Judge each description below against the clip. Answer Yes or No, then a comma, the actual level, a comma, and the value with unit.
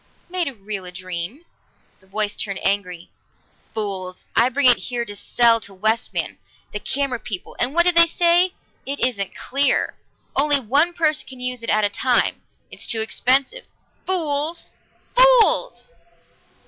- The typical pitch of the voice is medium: No, very high, 250 Hz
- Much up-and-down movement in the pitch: Yes, wide, 6.7 semitones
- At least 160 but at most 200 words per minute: No, average, 150 wpm